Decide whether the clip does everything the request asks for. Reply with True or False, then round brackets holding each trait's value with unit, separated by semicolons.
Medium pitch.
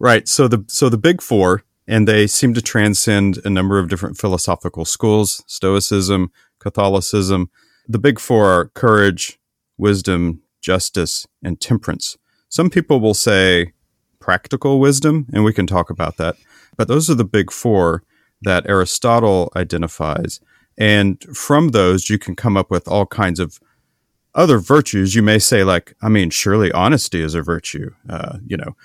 False (100 Hz)